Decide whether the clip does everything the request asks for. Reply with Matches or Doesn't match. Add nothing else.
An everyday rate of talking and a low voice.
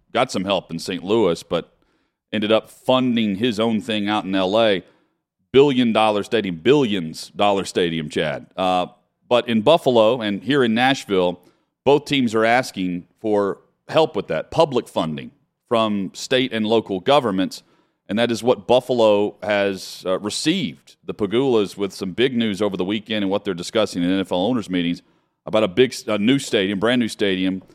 Matches